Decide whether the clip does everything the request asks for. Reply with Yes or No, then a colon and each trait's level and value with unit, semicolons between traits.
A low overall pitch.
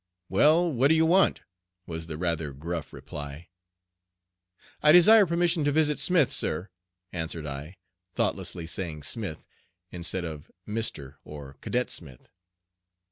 Yes: very low, 90 Hz